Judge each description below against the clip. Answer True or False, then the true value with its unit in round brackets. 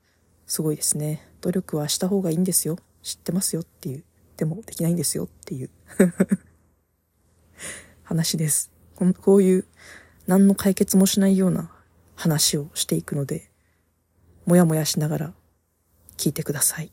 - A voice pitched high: False (155 Hz)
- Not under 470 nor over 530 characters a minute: False (300 characters per minute)